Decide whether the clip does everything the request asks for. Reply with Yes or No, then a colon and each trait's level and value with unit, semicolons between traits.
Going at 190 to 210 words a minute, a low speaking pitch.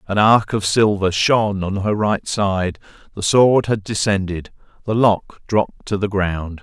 No: average, 170 wpm; low, 100 Hz